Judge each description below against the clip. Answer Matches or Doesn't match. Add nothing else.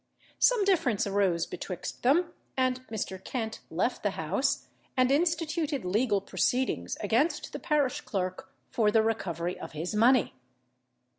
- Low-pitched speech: Doesn't match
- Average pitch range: Doesn't match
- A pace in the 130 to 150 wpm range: Matches